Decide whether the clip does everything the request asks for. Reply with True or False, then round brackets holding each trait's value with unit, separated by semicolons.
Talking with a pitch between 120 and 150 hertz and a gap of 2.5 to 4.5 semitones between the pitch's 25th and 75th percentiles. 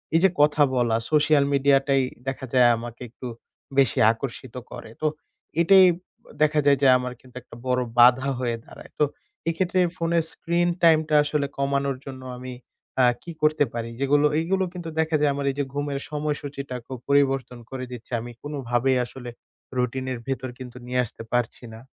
True (135 Hz; 3.1 semitones)